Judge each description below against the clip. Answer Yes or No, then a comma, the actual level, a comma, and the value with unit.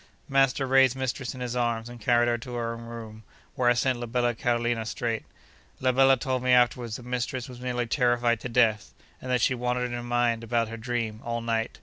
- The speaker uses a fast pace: Yes, fast, 225 wpm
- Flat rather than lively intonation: Yes, narrow, 1.3 semitones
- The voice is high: No, low, 120 Hz